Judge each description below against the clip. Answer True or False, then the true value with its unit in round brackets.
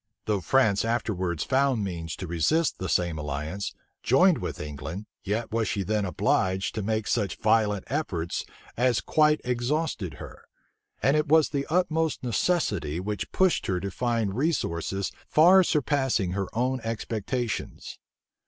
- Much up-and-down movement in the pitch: True (6.5 semitones)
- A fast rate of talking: False (145 wpm)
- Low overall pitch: True (110 Hz)